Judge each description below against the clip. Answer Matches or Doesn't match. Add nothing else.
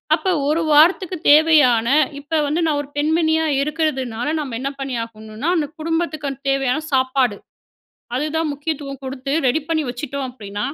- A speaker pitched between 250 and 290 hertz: Matches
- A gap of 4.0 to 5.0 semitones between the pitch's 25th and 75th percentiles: Doesn't match